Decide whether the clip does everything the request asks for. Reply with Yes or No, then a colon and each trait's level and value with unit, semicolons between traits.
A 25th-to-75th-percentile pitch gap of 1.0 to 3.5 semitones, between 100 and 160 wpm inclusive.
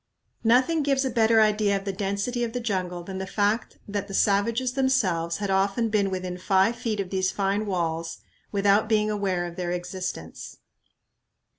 No: average, 3.0 semitones; average, 175 wpm